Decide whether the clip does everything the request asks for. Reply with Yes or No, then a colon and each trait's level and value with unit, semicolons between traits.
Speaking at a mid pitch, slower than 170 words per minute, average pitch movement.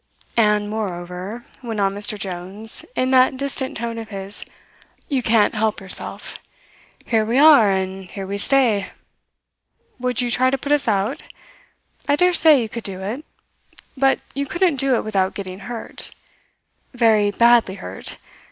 No: high, 220 Hz; average, 155 wpm; average, 4.6 semitones